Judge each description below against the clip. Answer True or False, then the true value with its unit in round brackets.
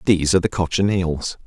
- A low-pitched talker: True (90 Hz)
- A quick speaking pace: False (165 wpm)